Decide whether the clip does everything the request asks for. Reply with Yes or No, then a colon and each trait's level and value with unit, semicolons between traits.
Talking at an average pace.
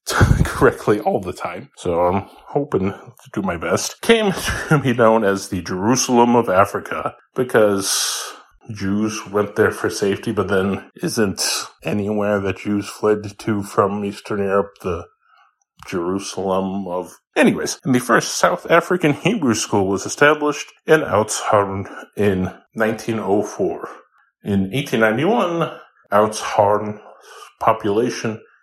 No: slow, 120 wpm